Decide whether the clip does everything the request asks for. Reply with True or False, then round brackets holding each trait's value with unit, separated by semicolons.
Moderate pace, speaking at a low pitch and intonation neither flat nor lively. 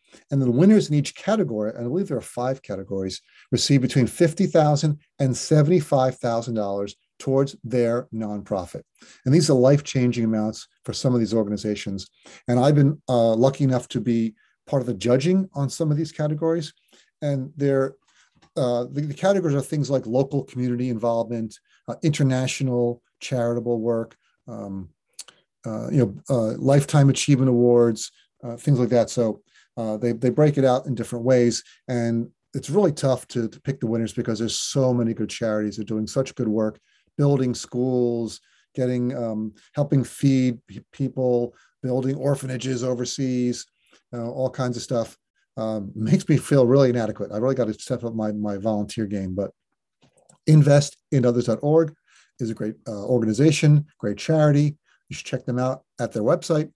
True (165 wpm; 125 Hz; 3.4 semitones)